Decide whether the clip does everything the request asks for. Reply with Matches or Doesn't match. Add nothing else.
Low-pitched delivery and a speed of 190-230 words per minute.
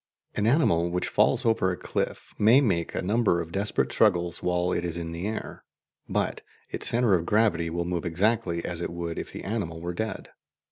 Matches